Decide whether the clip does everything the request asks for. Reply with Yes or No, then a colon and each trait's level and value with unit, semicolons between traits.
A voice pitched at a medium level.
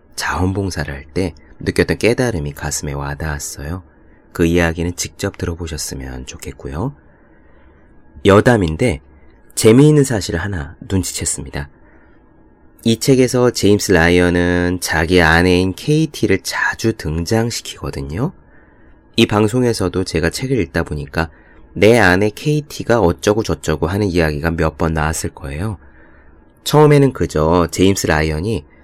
No: very low, 85 Hz